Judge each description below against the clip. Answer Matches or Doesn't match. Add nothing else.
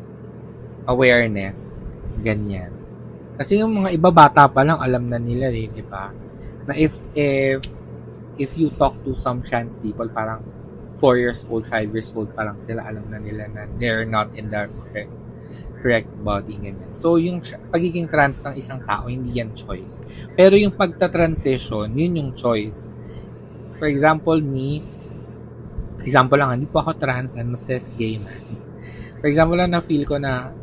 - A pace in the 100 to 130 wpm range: Doesn't match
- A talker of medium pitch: Doesn't match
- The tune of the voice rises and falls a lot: Doesn't match